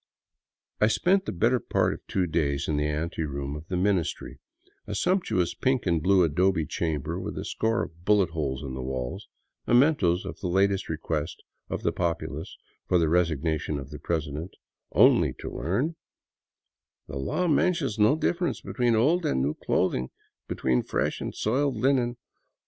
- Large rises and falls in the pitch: Yes, wide, 7.2 semitones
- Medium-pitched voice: No, very low, 85 Hz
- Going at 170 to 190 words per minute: Yes, average, 175 wpm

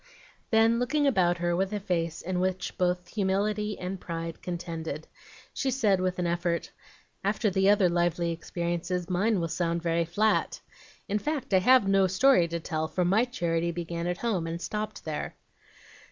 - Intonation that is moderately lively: Yes, average, 3.5 semitones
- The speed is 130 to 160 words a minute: No, average, 170 wpm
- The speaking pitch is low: No, medium, 180 Hz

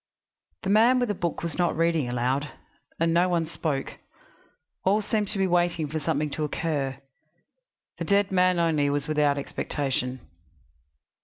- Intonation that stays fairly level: No, average, 4.2 semitones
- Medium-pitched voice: Yes, medium, 165 Hz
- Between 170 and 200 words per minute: No, average, 155 wpm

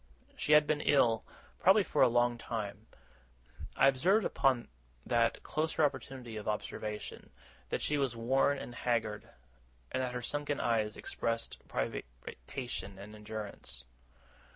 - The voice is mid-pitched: No, low, 120 Hz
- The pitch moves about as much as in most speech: Yes, average, 4.2 semitones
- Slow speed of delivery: Yes, slow, 130 wpm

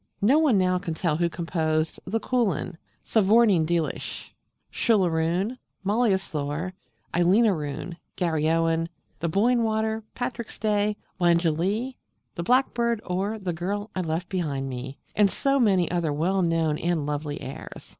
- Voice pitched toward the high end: No, medium, 180 Hz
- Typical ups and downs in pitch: Yes, average, 4.8 semitones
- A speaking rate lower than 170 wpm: Yes, average, 145 wpm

